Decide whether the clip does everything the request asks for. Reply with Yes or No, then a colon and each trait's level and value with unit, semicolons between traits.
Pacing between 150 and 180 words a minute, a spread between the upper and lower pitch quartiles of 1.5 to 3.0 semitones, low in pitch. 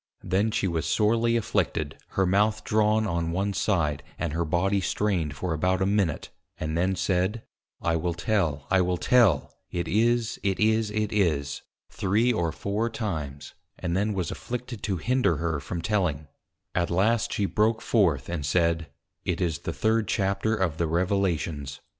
No: average, 170 wpm; average, 4.3 semitones; very low, 95 Hz